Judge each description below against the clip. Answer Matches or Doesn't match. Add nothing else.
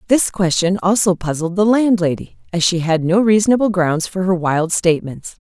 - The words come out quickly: Doesn't match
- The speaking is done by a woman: Matches